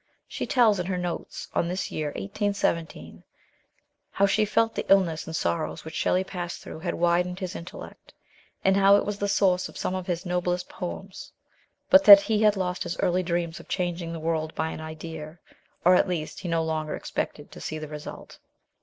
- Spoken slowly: No, average, 200 wpm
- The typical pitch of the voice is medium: Yes, medium, 180 Hz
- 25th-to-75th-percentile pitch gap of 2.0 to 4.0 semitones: Yes, average, 3.0 semitones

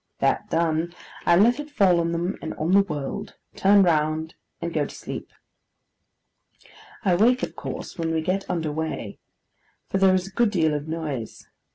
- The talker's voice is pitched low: No, medium, 170 Hz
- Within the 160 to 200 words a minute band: Yes, average, 180 wpm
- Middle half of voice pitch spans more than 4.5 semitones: No, average, 3.5 semitones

